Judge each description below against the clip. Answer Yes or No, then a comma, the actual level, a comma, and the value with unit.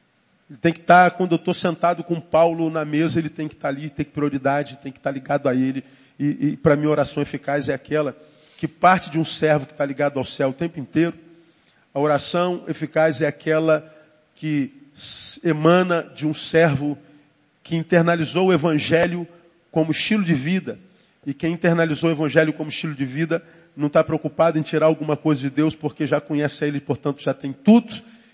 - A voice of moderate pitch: Yes, medium, 155 Hz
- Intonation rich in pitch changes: No, narrow, 2.3 semitones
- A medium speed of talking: No, fast, 200 wpm